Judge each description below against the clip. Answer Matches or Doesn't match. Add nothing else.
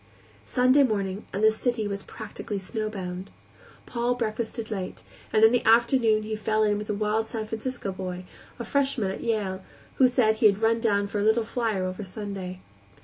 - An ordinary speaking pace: Matches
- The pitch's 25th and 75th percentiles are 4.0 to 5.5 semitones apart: Doesn't match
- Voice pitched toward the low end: Doesn't match